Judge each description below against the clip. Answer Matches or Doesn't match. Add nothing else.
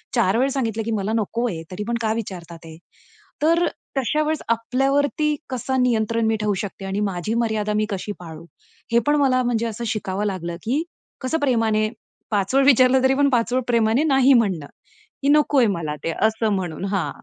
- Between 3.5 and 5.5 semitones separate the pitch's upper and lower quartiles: Matches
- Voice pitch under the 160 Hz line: Doesn't match